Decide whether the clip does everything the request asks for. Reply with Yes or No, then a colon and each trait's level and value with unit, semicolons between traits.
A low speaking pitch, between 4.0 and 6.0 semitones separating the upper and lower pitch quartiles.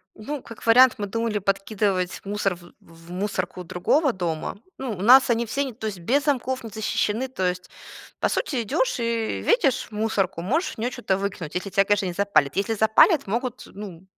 No: high, 210 Hz; average, 4.5 semitones